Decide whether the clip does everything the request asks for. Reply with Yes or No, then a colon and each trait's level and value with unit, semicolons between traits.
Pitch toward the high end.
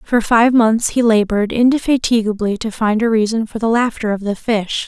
Yes: high, 225 Hz